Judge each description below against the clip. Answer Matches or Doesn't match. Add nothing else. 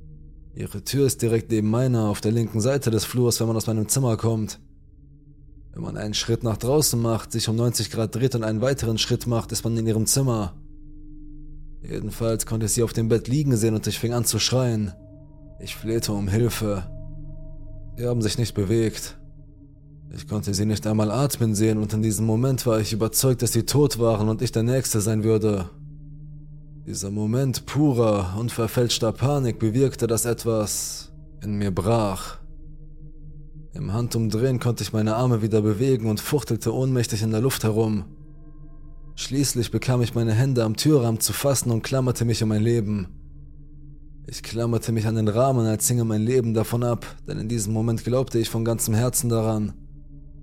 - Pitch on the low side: Matches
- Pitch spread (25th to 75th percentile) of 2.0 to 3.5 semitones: Matches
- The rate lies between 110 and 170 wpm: Doesn't match